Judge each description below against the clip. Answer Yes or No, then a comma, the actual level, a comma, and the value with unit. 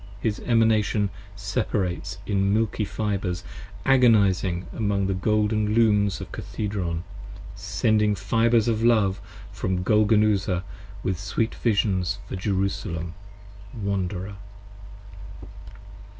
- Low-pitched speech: Yes, low, 100 Hz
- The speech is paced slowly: Yes, slow, 95 wpm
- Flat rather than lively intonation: Yes, narrow, 2.3 semitones